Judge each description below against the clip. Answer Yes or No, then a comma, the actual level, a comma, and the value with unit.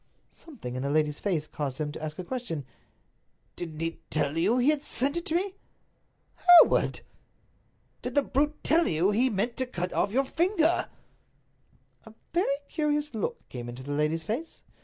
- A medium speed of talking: Yes, average, 180 wpm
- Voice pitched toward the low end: No, high, 220 Hz